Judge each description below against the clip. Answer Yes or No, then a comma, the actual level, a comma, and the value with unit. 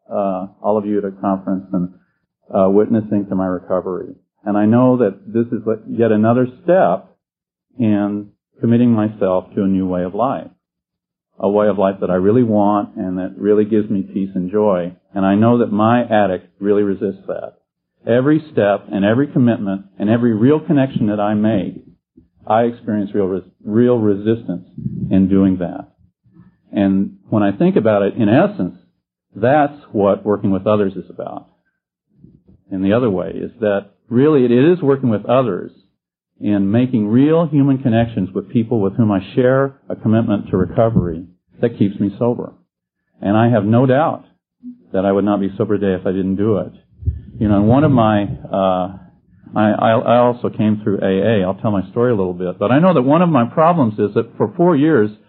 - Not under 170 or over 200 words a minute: Yes, average, 185 wpm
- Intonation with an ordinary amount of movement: Yes, average, 3.5 semitones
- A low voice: Yes, low, 105 Hz